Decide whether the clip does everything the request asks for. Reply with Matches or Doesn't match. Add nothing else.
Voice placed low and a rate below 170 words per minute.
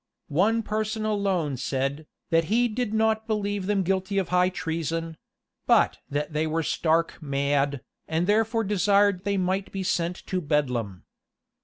Doesn't match